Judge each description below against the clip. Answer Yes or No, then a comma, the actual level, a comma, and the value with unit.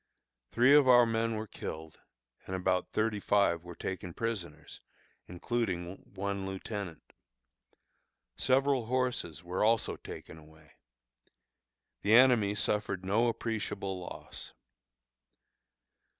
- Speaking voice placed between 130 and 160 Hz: No, low, 100 Hz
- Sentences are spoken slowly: Yes, slow, 105 wpm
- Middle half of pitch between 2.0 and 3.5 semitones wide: No, average, 4.4 semitones